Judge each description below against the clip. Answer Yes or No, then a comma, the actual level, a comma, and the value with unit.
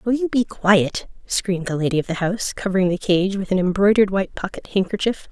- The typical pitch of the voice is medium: No, high, 195 Hz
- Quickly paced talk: Yes, fast, 215 wpm